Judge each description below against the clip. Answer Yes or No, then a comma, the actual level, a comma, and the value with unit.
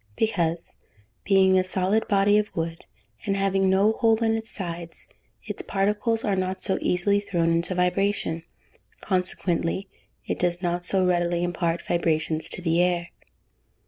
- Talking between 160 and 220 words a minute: No, average, 150 wpm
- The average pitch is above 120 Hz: Yes, medium, 185 Hz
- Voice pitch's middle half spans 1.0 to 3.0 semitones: Yes, narrow, 2.5 semitones